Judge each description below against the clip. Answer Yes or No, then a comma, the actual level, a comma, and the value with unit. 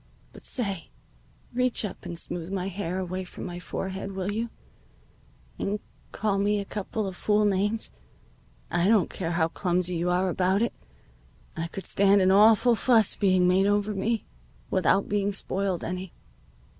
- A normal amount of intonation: No, narrow, 2.3 semitones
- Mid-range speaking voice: No, high, 195 Hz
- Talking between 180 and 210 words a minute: No, average, 160 wpm